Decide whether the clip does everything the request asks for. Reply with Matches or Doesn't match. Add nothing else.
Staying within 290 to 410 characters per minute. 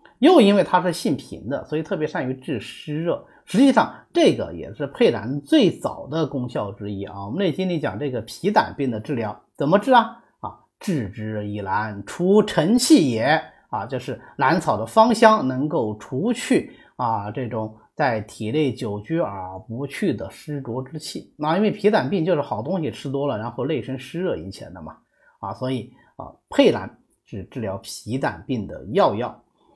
Doesn't match